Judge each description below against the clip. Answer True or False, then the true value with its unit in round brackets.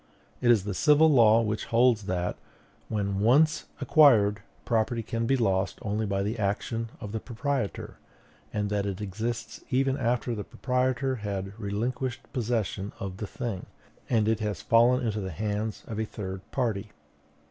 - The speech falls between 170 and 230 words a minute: False (160 wpm)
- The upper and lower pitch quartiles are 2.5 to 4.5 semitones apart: True (3.0 semitones)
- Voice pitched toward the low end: True (110 Hz)